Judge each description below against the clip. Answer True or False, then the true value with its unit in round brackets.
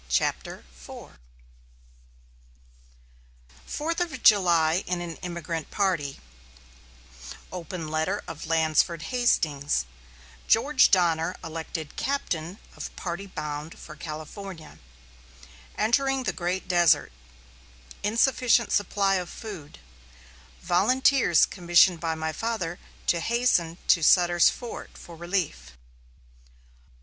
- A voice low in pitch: False (175 Hz)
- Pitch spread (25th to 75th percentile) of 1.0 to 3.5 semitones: False (4.3 semitones)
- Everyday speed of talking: False (100 wpm)